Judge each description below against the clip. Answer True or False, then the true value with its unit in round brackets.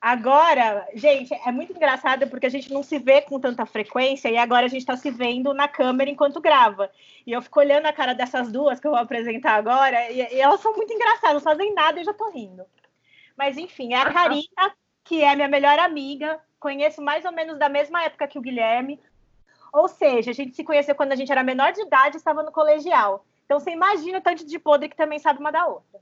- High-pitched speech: True (285 Hz)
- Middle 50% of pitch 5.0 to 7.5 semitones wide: False (3.5 semitones)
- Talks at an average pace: False (235 wpm)